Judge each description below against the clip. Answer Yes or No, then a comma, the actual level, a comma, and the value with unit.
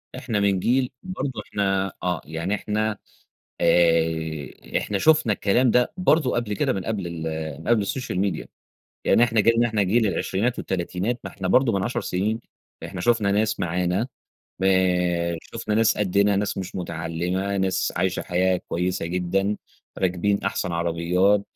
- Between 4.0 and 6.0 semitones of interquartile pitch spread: No, average, 3.5 semitones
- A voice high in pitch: No, very low, 95 Hz